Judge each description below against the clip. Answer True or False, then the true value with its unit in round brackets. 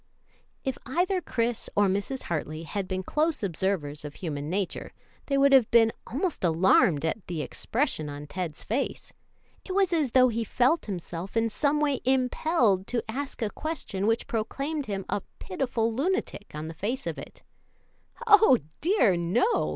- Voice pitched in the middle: False (225 Hz)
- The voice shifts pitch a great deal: True (7.0 semitones)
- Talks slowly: False (165 wpm)